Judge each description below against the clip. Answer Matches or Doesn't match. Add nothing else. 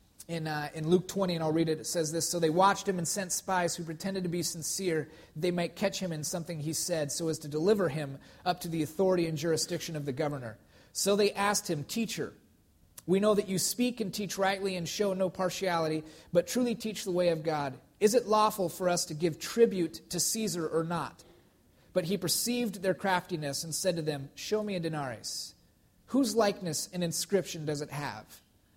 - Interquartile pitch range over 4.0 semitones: Doesn't match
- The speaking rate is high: Matches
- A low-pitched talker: Doesn't match